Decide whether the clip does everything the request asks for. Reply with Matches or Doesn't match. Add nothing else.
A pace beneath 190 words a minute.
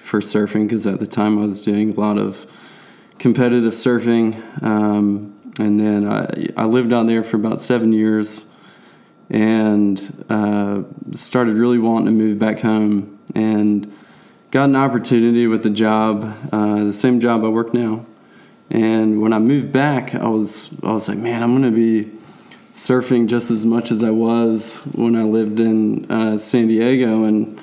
Matches